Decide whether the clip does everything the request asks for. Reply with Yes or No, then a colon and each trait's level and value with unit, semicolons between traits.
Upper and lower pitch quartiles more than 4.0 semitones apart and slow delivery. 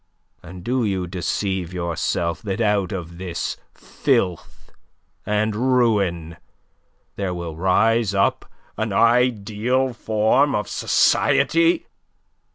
Yes: average, 4.5 semitones; slow, 100 wpm